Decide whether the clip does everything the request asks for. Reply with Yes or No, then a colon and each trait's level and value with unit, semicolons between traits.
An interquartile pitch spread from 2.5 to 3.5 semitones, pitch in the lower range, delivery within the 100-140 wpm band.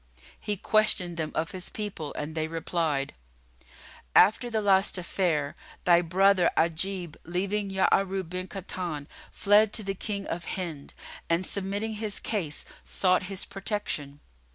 No: average, 3.2 semitones; medium, 185 Hz; slow, 135 wpm